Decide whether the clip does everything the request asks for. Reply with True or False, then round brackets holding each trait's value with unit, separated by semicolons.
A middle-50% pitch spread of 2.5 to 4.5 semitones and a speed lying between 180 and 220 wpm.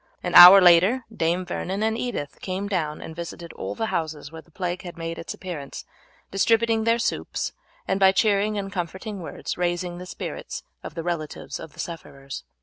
True (3.2 semitones; 185 wpm)